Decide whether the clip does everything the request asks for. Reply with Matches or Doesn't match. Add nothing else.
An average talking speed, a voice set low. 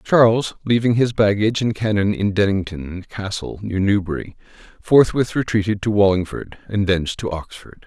Matches